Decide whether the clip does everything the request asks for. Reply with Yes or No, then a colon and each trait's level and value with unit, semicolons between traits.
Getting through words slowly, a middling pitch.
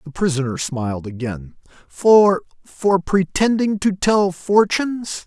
Yes: slow, 105 wpm; medium, 170 Hz